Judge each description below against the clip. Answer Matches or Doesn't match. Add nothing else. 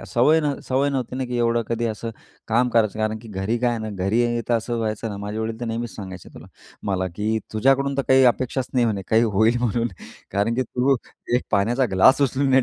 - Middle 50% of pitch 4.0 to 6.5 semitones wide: Doesn't match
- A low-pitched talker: Matches